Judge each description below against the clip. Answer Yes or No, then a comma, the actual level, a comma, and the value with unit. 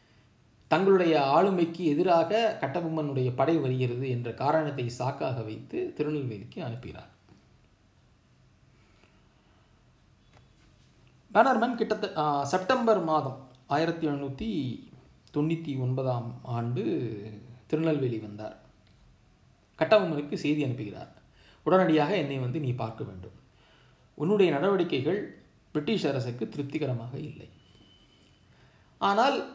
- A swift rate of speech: No, average, 80 wpm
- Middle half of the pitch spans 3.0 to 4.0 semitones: No, wide, 5.4 semitones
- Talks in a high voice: No, medium, 140 Hz